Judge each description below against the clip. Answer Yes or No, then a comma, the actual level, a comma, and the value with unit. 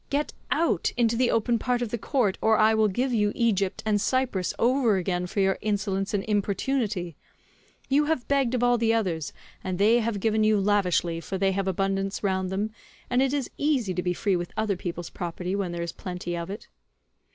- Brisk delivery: Yes, fast, 210 wpm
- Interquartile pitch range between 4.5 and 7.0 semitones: No, average, 3.9 semitones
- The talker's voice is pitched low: No, high, 205 Hz